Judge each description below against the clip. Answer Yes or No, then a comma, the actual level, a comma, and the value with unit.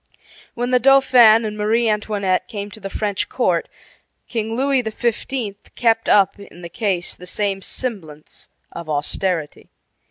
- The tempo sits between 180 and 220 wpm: No, average, 140 wpm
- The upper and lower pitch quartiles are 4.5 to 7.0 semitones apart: No, average, 3.4 semitones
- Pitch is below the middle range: No, high, 210 Hz